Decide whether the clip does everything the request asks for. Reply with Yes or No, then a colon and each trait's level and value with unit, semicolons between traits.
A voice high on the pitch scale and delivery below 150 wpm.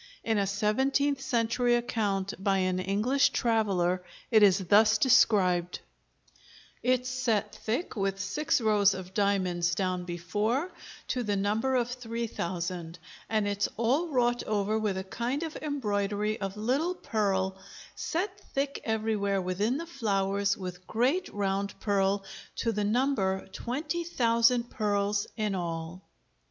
Yes: high, 210 Hz; slow, 135 wpm